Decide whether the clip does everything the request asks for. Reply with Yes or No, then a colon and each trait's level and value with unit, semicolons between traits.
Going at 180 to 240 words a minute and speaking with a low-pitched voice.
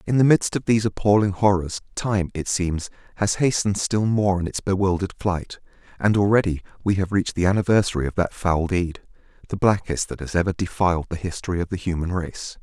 Yes: average, 195 wpm; very low, 95 Hz